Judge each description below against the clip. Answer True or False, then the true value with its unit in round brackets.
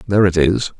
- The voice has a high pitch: False (95 Hz)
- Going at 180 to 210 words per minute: False (230 wpm)